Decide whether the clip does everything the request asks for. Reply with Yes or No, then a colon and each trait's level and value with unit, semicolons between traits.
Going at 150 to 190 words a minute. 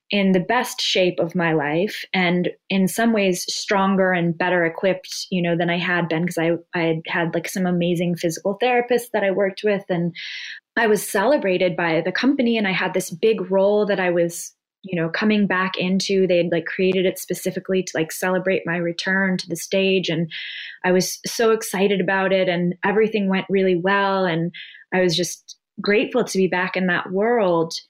No: average, 200 wpm